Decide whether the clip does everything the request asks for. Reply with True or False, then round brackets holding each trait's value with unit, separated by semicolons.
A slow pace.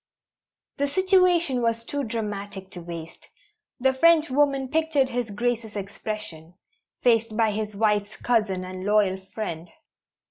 True (120 wpm)